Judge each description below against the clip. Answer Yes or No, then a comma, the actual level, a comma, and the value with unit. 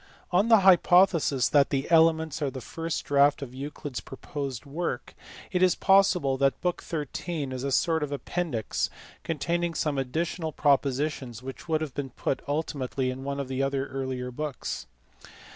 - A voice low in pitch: No, medium, 145 Hz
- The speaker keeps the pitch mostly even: No, average, 3.5 semitones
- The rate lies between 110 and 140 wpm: No, average, 170 wpm